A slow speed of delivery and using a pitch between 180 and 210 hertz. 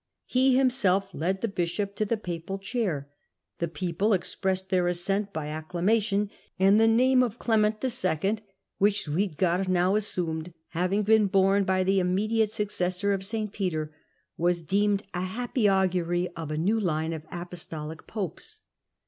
No: average, 155 wpm; high, 190 Hz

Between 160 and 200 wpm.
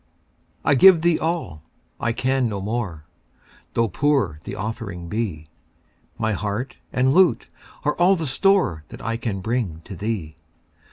No: average, 150 wpm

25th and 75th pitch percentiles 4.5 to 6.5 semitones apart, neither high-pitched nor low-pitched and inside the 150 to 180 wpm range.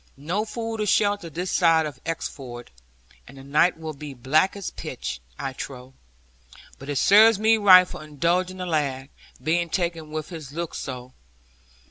Yes: average, 4.9 semitones; medium, 160 Hz; average, 165 wpm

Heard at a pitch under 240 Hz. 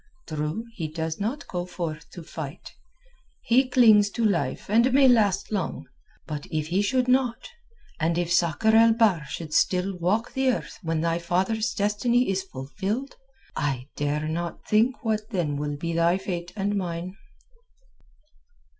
Yes: medium, 185 Hz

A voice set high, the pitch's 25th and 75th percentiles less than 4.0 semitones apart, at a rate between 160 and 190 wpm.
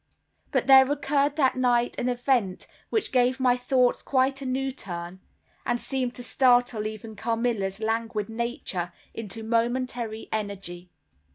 No: high, 240 Hz; average, 3.0 semitones; average, 140 wpm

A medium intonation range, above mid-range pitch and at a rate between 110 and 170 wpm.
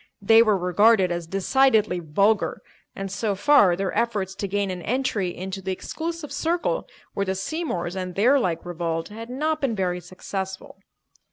Yes: average, 4.2 semitones; high, 195 Hz; average, 165 wpm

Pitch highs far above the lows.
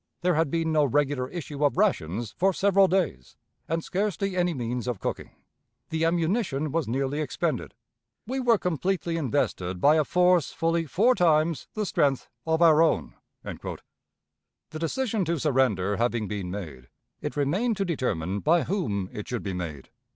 Yes: wide, 6.4 semitones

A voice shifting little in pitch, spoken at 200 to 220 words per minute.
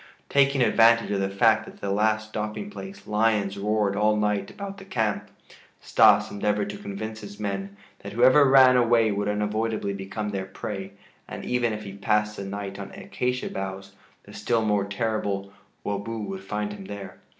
No: narrow, 2.1 semitones; average, 180 wpm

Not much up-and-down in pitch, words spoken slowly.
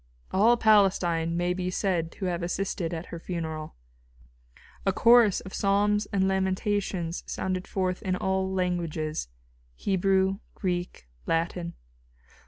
Yes: narrow, 2.3 semitones; slow, 120 wpm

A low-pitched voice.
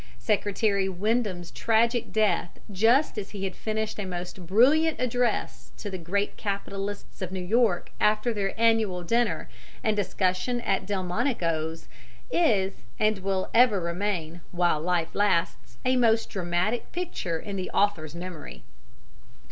No: high, 200 Hz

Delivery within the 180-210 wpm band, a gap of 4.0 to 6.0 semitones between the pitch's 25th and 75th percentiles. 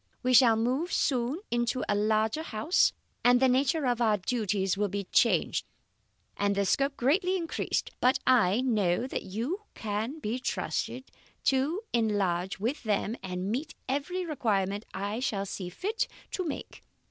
No: average, 155 wpm; average, 5.1 semitones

